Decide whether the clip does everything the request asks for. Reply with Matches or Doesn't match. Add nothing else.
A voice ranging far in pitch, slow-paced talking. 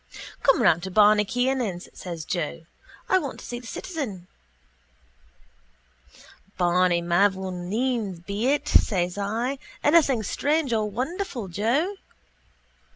Matches